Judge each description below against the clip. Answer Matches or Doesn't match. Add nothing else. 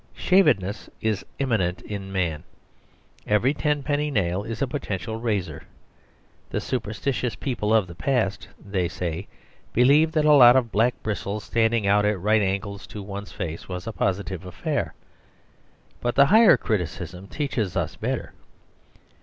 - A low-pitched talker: Matches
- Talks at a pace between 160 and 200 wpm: Doesn't match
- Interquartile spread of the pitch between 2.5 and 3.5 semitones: Doesn't match